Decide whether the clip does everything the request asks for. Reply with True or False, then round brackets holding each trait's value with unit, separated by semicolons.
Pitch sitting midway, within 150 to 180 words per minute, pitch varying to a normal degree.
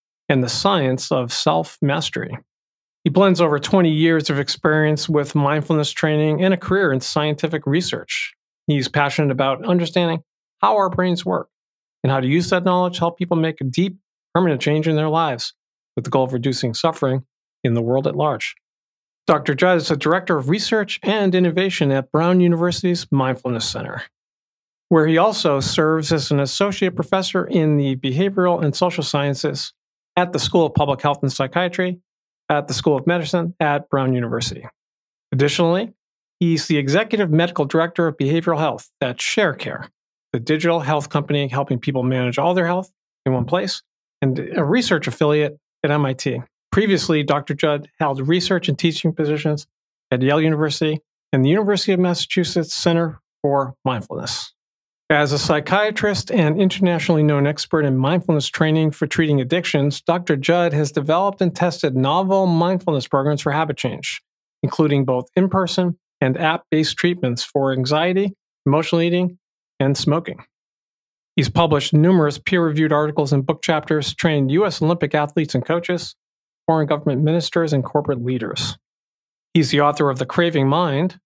True (155 Hz; 160 wpm; 3.5 semitones)